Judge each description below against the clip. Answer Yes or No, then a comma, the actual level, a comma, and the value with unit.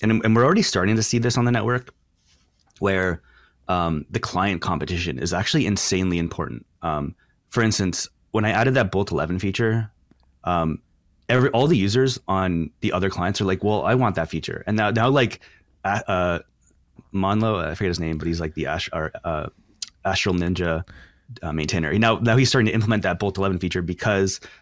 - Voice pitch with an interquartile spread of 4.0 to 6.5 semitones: Yes, average, 4.3 semitones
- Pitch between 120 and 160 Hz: No, very low, 95 Hz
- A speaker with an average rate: Yes, average, 190 wpm